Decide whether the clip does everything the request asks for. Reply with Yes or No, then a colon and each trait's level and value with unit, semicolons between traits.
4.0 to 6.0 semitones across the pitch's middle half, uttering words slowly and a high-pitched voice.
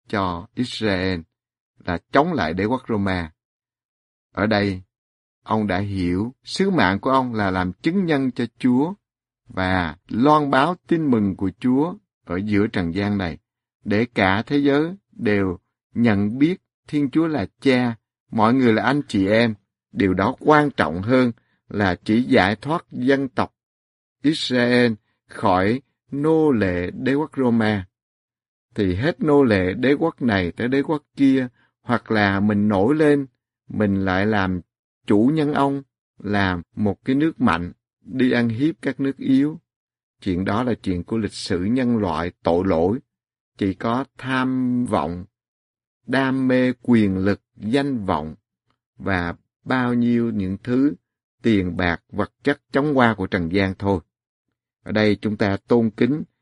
No: average, 5.3 semitones; slow, 155 wpm; low, 115 Hz